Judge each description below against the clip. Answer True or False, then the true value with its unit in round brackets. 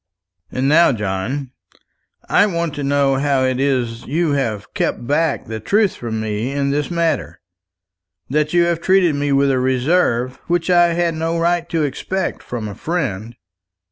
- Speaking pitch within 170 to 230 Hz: False (145 Hz)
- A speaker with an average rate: True (170 wpm)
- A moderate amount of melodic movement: True (4.8 semitones)